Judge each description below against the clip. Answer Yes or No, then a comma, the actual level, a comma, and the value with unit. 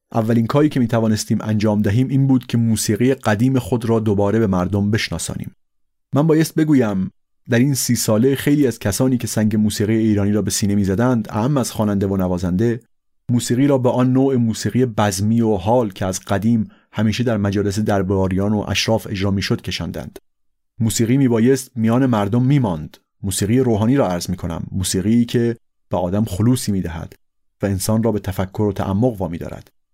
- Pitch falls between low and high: No, low, 110 Hz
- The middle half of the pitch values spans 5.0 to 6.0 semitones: No, average, 3.5 semitones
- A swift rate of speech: Yes, fast, 185 wpm